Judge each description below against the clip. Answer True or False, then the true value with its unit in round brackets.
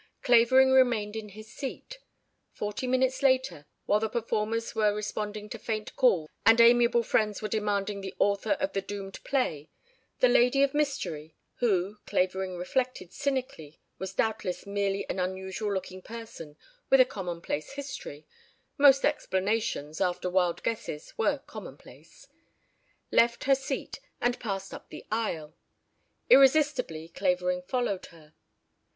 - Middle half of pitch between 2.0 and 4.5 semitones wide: False (5.0 semitones)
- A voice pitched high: True (210 Hz)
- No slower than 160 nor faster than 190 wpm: False (135 wpm)